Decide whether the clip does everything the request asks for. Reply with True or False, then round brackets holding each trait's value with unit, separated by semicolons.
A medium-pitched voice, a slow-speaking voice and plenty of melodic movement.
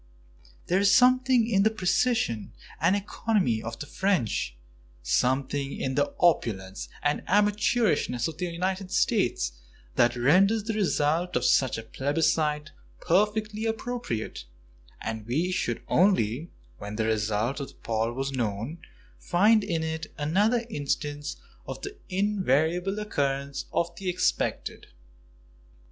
True (160 Hz; 125 wpm; 7.5 semitones)